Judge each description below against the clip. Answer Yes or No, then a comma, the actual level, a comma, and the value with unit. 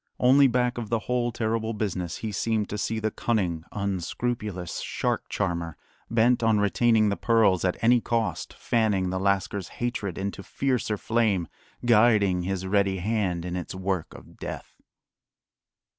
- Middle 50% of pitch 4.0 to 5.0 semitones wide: No, average, 3.6 semitones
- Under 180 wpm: Yes, average, 150 wpm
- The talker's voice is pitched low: Yes, low, 105 Hz